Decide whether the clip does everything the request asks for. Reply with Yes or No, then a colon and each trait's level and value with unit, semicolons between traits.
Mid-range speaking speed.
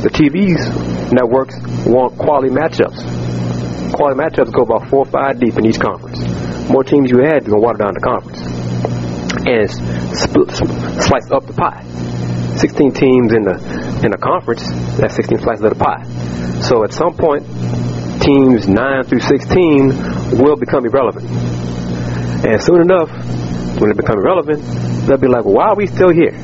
Yes: average, 165 wpm